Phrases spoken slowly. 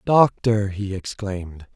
Yes: slow, 105 wpm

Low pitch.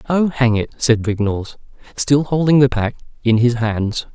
Yes: low, 125 Hz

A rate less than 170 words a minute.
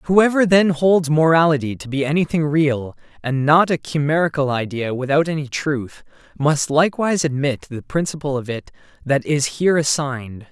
Yes: average, 155 wpm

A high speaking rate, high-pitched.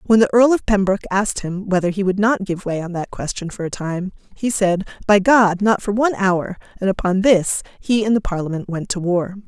Yes: fast, 235 wpm; high, 195 Hz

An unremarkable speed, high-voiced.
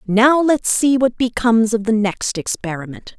Yes: average, 170 wpm; high, 230 Hz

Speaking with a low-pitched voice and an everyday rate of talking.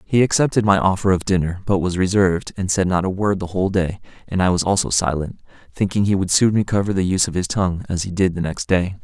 No: very low, 95 Hz; fast, 250 wpm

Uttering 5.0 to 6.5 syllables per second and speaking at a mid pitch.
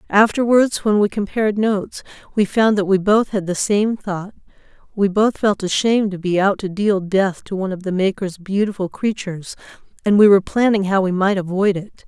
No: 5.4 syllables/s; high, 200 Hz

